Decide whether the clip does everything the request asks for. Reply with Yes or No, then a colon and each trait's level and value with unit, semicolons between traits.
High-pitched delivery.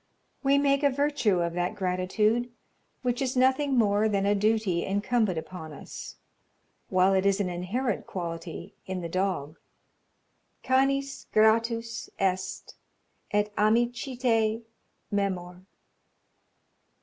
Yes: high, 210 Hz